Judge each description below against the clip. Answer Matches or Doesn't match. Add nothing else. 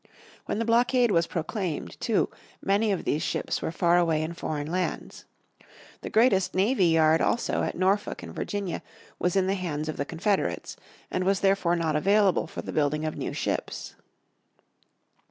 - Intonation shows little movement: Doesn't match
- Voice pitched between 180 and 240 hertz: Matches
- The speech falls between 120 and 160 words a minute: Doesn't match